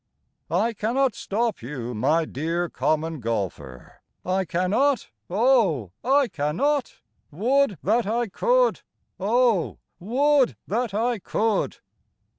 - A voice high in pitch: Yes, high, 210 Hz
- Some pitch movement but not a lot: No, wide, 7.3 semitones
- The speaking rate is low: Yes, slow, 105 wpm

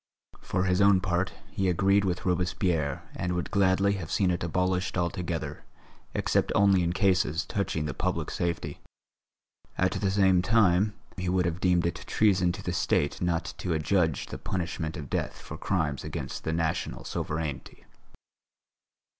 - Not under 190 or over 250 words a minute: No, average, 155 wpm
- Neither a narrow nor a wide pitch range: No, narrow, 2.1 semitones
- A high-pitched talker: No, very low, 90 Hz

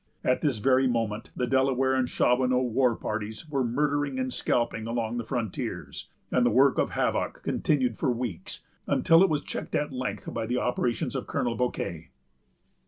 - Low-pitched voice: Yes, low, 125 Hz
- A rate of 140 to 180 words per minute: Yes, average, 170 wpm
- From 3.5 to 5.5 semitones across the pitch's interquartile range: No, narrow, 2.4 semitones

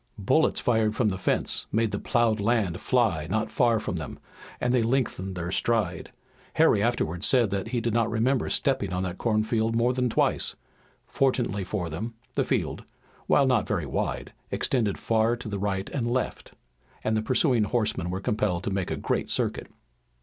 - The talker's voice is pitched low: Yes, low, 110 Hz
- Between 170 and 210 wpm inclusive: Yes, average, 180 wpm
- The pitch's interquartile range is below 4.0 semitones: Yes, average, 3.5 semitones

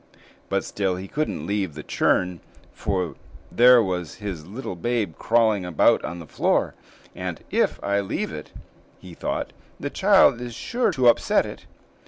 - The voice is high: No, low, 100 Hz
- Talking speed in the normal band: Yes, average, 160 wpm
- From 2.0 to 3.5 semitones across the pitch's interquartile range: No, average, 4.9 semitones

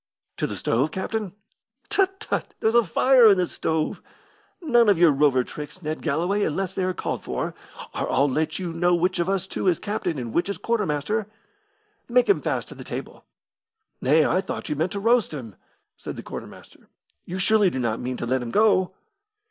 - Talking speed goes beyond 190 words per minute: Yes, average, 200 wpm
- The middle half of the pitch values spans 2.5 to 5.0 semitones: No, wide, 5.6 semitones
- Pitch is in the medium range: Yes, medium, 180 Hz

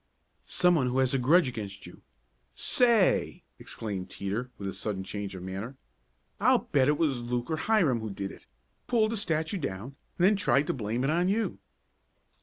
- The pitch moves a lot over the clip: Yes, wide, 8.4 semitones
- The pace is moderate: Yes, average, 190 wpm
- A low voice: Yes, low, 130 Hz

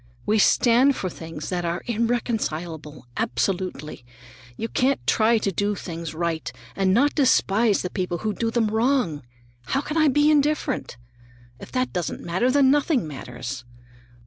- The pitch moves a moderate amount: No, wide, 7.1 semitones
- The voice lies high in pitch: Yes, high, 210 Hz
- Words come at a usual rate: Yes, average, 150 wpm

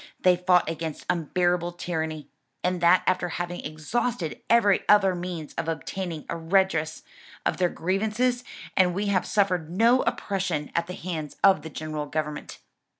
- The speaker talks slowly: No, average, 150 wpm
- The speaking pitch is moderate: Yes, medium, 175 Hz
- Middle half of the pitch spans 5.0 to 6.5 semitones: No, average, 3.1 semitones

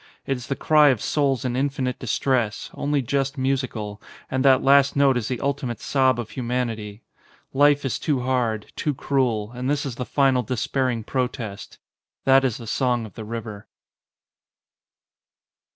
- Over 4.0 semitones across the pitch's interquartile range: No, average, 2.8 semitones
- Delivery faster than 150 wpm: Yes, average, 160 wpm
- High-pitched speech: No, low, 130 Hz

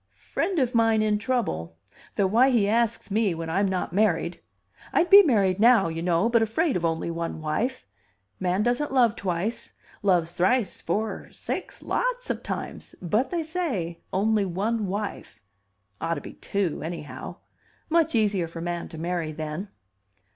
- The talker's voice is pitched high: Yes, high, 205 Hz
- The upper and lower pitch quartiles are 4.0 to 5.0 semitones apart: No, wide, 5.6 semitones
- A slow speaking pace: No, average, 160 wpm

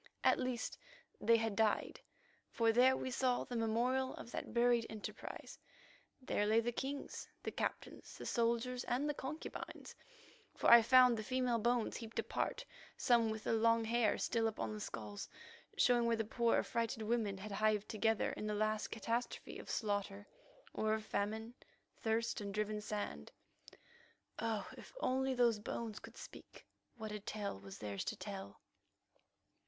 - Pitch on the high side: Yes, high, 225 Hz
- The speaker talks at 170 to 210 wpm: No, average, 160 wpm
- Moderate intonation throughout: No, narrow, 2.2 semitones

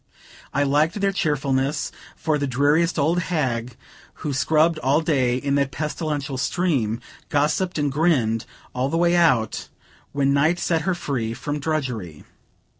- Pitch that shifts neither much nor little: Yes, average, 3.4 semitones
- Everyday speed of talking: Yes, average, 145 wpm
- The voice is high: No, medium, 145 Hz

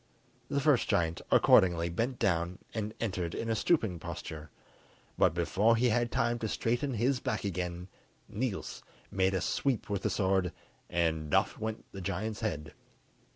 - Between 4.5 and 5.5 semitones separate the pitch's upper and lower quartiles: Yes, average, 4.9 semitones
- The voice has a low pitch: Yes, low, 100 Hz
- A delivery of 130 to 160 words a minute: Yes, average, 155 wpm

